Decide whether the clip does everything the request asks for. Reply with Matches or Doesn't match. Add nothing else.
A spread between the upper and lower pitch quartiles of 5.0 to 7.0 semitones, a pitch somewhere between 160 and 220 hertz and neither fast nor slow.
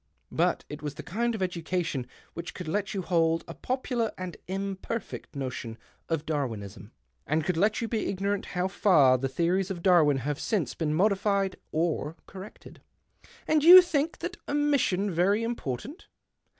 Matches